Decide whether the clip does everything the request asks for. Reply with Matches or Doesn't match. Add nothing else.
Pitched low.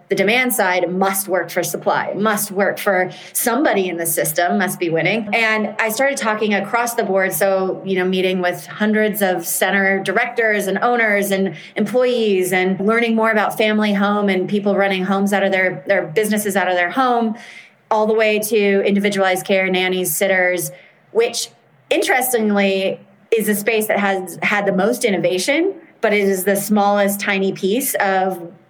Doesn't match